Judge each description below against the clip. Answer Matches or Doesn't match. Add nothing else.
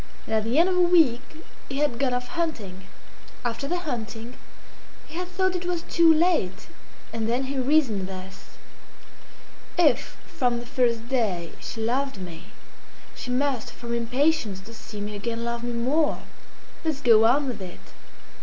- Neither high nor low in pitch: Doesn't match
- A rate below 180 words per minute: Matches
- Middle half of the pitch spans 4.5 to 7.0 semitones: Matches